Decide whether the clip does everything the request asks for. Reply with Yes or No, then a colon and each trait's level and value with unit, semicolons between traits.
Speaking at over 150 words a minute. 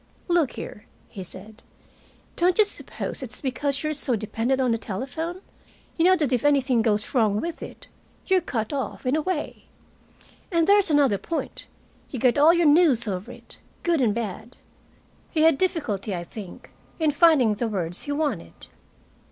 Yes: average, 170 wpm